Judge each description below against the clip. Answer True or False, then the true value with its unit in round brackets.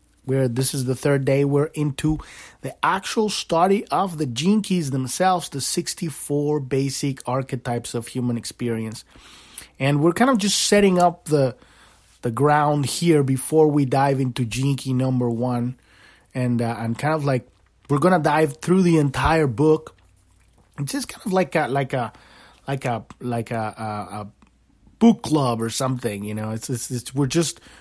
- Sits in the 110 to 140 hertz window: True (135 Hz)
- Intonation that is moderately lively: True (4.3 semitones)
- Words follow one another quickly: False (170 wpm)